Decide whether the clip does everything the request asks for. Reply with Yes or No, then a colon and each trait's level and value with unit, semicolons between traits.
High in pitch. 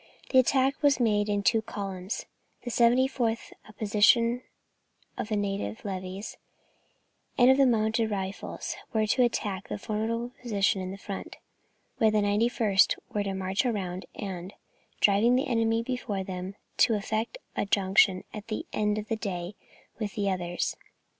Yes: high, 210 Hz